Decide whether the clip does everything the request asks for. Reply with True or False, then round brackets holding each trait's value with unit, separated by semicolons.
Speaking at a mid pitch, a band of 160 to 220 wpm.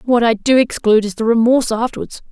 False (230 Hz; 205 wpm)